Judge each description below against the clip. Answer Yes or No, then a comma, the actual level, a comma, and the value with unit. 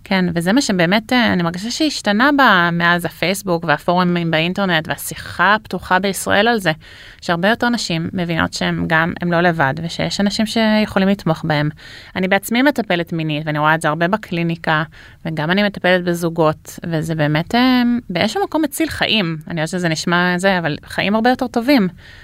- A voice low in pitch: No, medium, 175 Hz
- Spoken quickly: Yes, fast, 165 wpm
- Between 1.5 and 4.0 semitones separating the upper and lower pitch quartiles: No, average, 4.7 semitones